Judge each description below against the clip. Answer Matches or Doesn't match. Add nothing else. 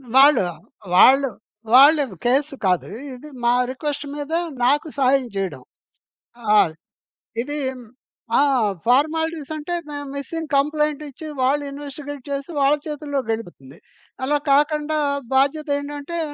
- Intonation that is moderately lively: Doesn't match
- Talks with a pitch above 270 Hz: Matches